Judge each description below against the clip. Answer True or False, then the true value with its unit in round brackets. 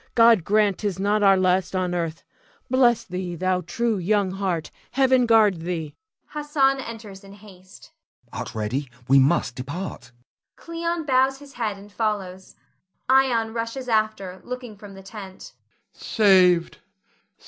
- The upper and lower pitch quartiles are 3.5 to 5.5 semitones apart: True (4.3 semitones)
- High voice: True (200 Hz)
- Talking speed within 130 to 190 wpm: True (145 wpm)